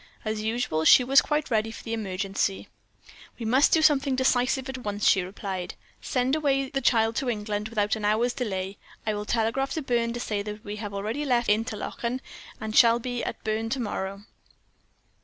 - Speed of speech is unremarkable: Yes, average, 190 wpm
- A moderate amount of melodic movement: Yes, average, 3.4 semitones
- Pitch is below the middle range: No, high, 225 Hz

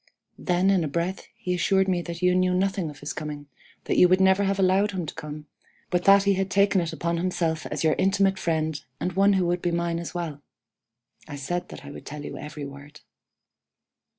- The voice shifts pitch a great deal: No, average, 3.3 semitones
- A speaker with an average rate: No, fast, 220 wpm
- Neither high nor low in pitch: Yes, medium, 175 Hz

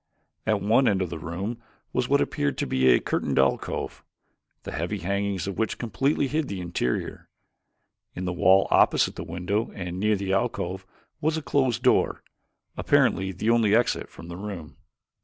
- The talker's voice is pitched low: Yes, low, 100 Hz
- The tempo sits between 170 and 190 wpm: Yes, average, 175 wpm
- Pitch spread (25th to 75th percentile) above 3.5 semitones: Yes, average, 4.4 semitones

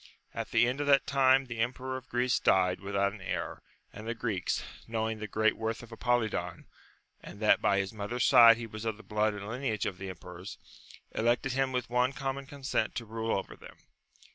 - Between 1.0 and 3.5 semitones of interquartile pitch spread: Yes, average, 3.2 semitones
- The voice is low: Yes, low, 115 Hz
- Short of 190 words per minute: No, fast, 205 wpm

